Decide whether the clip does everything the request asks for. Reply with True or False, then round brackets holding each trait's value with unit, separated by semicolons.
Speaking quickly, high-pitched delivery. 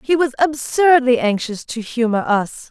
False (155 wpm; 255 Hz)